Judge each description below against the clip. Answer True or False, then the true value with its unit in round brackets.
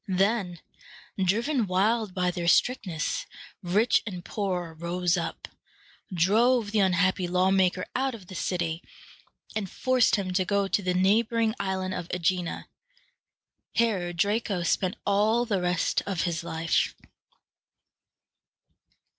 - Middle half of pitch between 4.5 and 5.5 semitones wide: False (3.2 semitones)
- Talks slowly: True (125 wpm)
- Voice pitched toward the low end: False (190 Hz)